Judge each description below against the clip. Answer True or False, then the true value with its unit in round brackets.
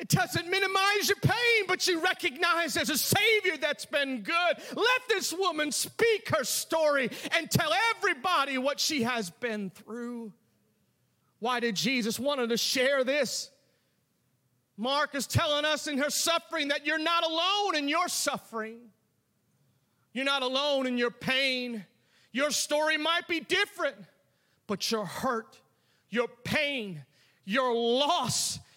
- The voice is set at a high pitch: True (285 Hz)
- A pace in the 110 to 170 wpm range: True (140 wpm)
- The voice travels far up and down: True (5.9 semitones)